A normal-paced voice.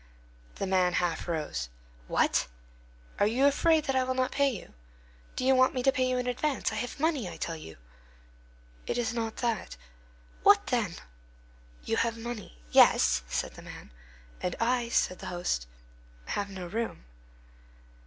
Yes: average, 165 wpm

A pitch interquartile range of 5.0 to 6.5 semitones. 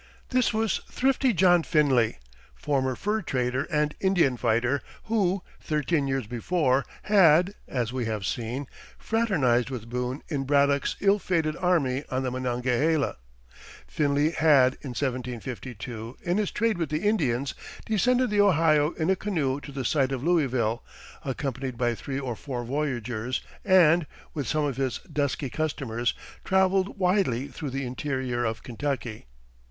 Yes: wide, 5.5 semitones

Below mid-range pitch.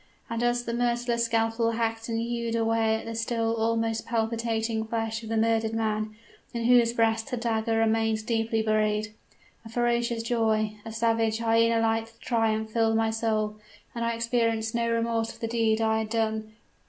No: high, 225 Hz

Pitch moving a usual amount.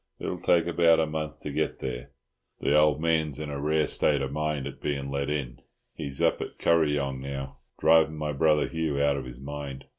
No: narrow, 2.0 semitones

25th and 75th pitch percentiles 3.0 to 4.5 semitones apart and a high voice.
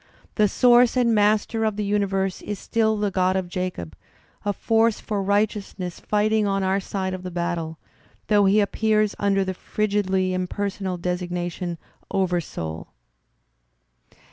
No: narrow, 2.4 semitones; high, 195 Hz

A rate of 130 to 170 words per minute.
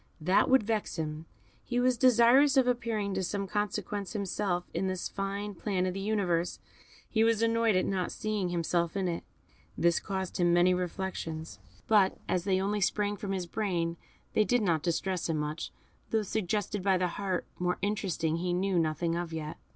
No: average, 180 wpm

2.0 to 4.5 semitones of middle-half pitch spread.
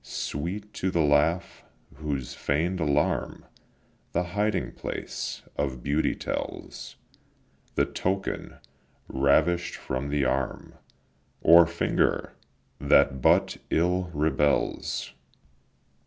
Yes: average, 3.7 semitones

